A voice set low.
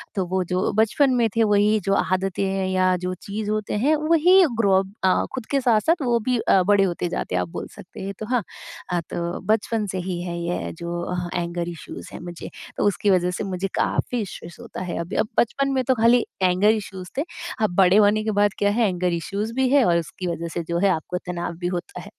No: high, 195 Hz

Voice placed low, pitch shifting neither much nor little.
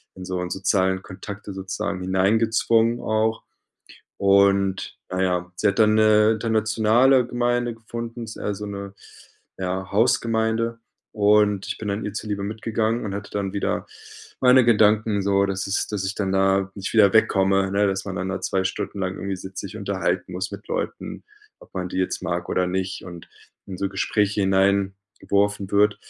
No: low, 100 Hz; narrow, 2.3 semitones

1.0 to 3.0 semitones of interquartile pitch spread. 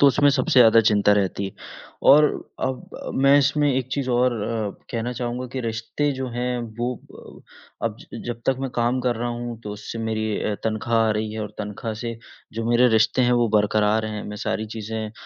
Yes: narrow, 2.5 semitones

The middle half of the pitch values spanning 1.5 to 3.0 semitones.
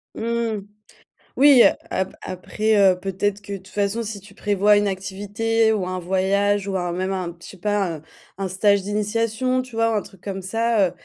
Yes: narrow, 2.6 semitones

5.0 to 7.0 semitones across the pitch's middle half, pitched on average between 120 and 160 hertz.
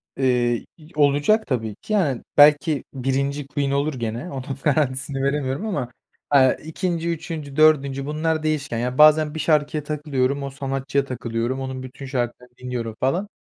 No: average, 2.7 semitones; medium, 140 Hz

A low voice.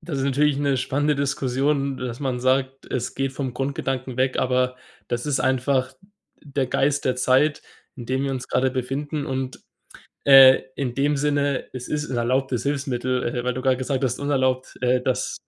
Yes: low, 130 Hz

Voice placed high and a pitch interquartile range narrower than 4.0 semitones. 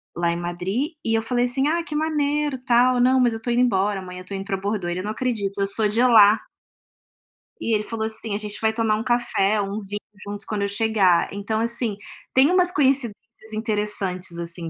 Yes: high, 220 Hz; average, 3.6 semitones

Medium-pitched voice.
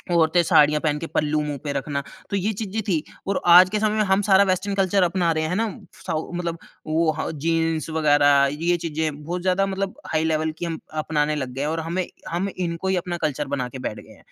Yes: medium, 165 Hz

